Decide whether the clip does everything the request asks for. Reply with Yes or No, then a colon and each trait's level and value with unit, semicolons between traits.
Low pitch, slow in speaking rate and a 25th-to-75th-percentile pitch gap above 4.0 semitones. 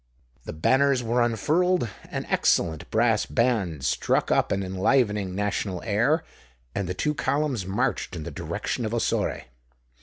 No: low, 115 Hz; average, 145 wpm; average, 5.3 semitones